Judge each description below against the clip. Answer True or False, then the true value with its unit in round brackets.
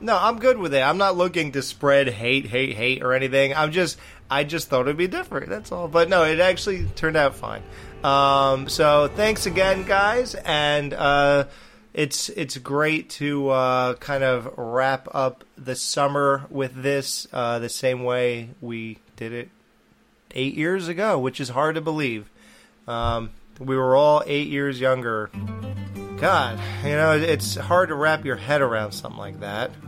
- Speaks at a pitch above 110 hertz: True (135 Hz)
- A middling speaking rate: True (175 wpm)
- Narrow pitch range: False (4.1 semitones)